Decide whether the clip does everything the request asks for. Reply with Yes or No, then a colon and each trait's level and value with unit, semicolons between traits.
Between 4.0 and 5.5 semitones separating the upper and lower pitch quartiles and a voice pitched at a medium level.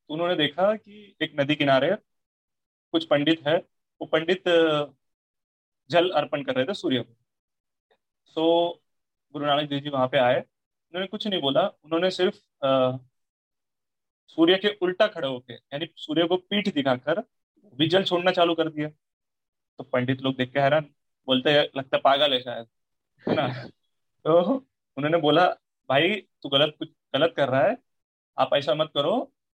Yes: average, 4.7 semitones; medium, 150 Hz